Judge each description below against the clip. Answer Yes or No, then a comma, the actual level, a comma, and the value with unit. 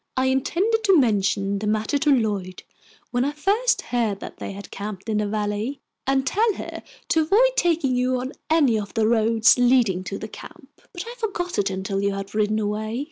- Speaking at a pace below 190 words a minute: No, average, 200 wpm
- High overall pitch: Yes, high, 235 Hz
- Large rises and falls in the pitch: Yes, wide, 6.3 semitones